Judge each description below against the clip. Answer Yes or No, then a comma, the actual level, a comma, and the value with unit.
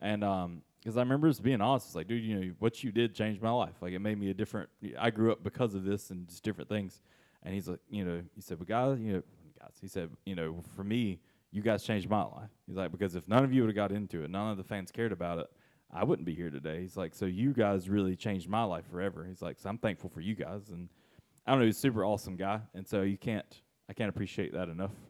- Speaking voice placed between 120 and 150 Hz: No, low, 100 Hz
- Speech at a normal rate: No, fast, 280 wpm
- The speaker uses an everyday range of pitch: Yes, average, 3.3 semitones